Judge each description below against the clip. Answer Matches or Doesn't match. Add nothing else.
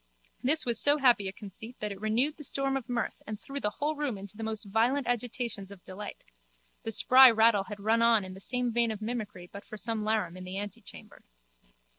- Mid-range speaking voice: Doesn't match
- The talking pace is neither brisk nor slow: Doesn't match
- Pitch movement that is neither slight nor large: Matches